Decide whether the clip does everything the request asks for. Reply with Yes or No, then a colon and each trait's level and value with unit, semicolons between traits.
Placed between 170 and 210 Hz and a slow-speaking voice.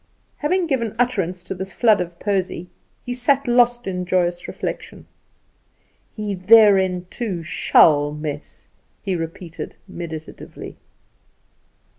Yes: high, 190 Hz; slow, 110 wpm